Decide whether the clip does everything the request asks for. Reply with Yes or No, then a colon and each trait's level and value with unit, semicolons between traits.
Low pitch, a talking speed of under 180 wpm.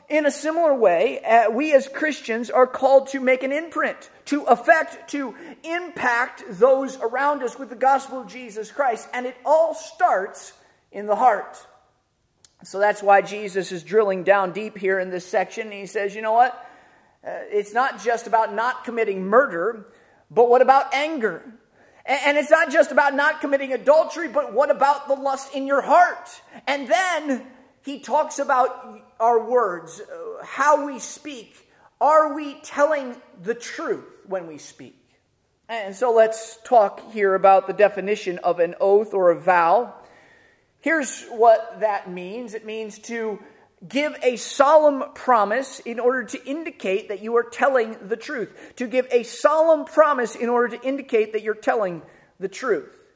No: very high, 255 Hz; average, 165 wpm